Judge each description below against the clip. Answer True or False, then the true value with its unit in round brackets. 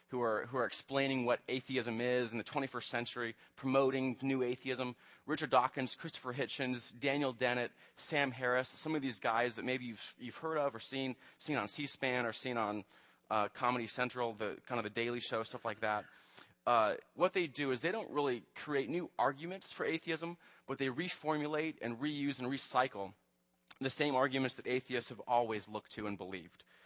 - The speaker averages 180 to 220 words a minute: True (190 wpm)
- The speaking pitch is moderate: False (130 Hz)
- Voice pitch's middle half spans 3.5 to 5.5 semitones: False (2.9 semitones)